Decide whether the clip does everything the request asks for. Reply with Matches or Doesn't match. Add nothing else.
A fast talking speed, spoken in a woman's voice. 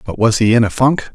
Doesn't match